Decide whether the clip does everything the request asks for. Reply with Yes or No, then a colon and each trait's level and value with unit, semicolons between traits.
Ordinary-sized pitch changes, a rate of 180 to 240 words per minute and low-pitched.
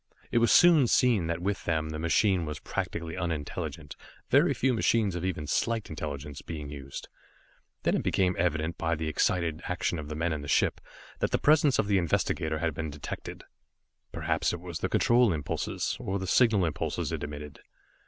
Yes: average, 4.3 semitones; average, 185 wpm; very low, 85 Hz